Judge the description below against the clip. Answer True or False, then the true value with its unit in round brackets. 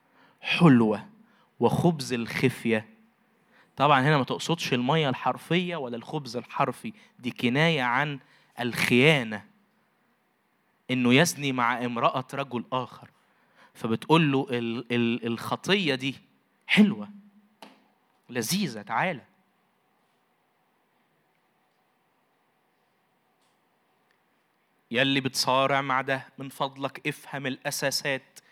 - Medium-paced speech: True (80 wpm)